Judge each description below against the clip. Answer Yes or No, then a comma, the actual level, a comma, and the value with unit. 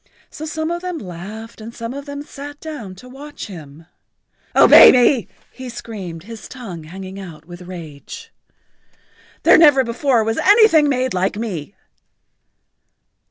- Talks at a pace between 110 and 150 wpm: Yes, average, 145 wpm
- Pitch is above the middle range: Yes, high, 230 Hz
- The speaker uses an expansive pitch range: Yes, wide, 7.4 semitones